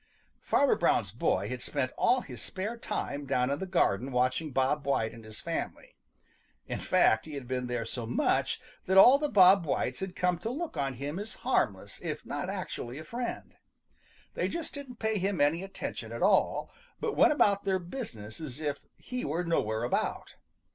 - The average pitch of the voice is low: No, medium, 155 Hz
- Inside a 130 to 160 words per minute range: No, average, 190 wpm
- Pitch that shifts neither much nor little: No, wide, 7.8 semitones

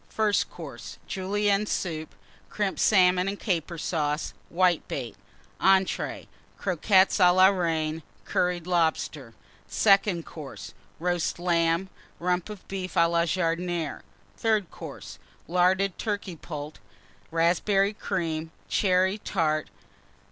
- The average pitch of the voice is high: No, medium, 180 Hz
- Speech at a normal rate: No, slow, 105 wpm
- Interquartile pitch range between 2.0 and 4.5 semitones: Yes, average, 2.7 semitones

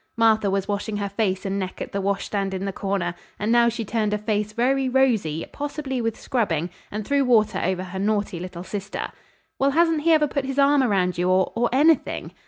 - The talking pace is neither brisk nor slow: No, fast, 210 wpm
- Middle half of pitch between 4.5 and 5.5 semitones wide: Yes, average, 5.1 semitones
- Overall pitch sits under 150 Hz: No, high, 210 Hz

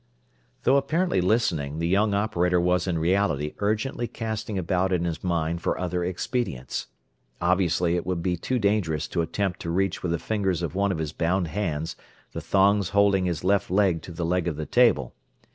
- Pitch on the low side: Yes, very low, 90 Hz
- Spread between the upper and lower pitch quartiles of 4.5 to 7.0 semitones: No, average, 3.2 semitones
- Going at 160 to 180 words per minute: No, average, 190 wpm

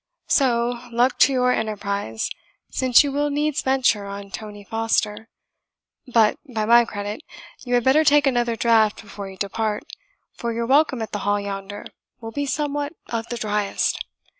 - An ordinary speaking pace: Yes, average, 165 wpm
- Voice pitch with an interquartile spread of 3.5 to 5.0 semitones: Yes, average, 3.8 semitones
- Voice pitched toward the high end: Yes, high, 230 Hz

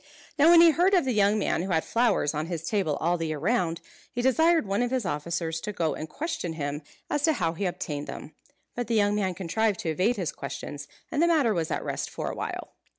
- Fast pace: Yes, fast, 245 wpm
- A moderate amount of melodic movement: No, wide, 7.1 semitones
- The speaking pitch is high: Yes, high, 200 Hz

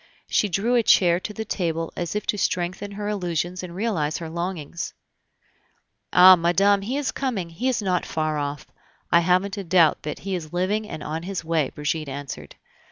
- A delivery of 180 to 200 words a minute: Yes, average, 190 wpm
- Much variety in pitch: No, average, 3.6 semitones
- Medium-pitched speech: Yes, medium, 180 Hz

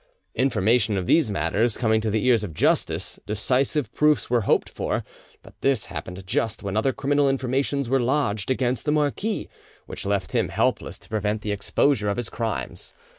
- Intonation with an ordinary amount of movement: Yes, average, 4.8 semitones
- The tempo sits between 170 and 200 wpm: Yes, average, 175 wpm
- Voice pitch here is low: Yes, low, 115 Hz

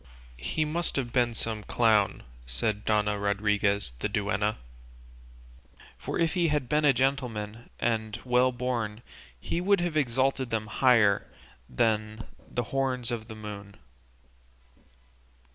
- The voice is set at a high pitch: No, low, 115 Hz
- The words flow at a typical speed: No, slow, 125 wpm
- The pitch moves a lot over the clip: No, average, 3.9 semitones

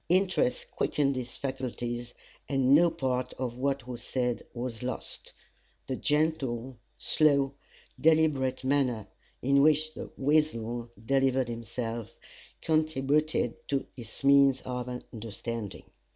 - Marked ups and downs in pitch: No, average, 2.9 semitones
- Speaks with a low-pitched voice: Yes, low, 130 Hz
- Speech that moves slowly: Yes, slow, 110 wpm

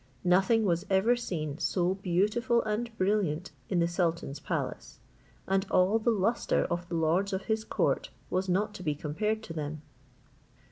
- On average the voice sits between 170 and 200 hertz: Yes, high, 190 Hz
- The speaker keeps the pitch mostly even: No, average, 3.8 semitones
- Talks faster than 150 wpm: Yes, average, 160 wpm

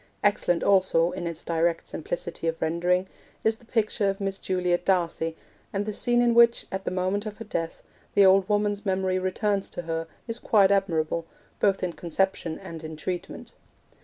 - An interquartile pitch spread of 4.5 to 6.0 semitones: No, average, 3.2 semitones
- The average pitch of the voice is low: No, high, 190 Hz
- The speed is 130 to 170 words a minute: No, average, 180 wpm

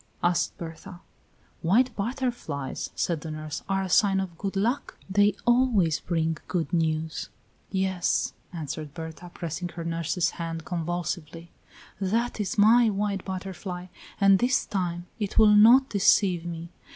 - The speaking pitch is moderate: Yes, medium, 180 Hz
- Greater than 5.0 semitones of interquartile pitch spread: No, average, 3.6 semitones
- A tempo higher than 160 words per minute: No, average, 140 wpm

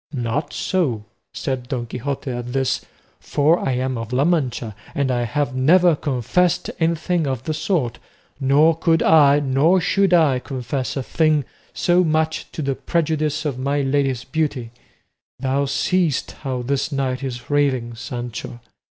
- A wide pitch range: No, average, 3.7 semitones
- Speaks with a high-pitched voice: No, medium, 140 Hz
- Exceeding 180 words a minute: No, average, 150 wpm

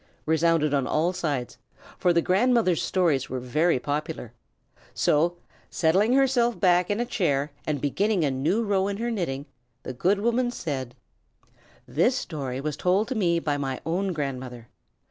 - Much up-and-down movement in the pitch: Yes, wide, 5.9 semitones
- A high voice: No, medium, 170 Hz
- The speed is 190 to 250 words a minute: No, average, 160 wpm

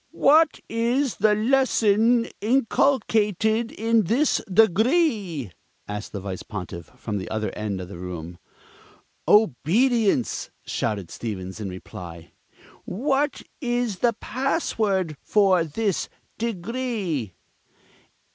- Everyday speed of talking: No, slow, 100 wpm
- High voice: Yes, high, 210 Hz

